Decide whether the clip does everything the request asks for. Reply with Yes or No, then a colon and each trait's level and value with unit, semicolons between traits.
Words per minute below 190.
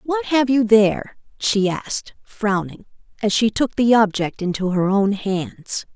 Yes: average, 160 wpm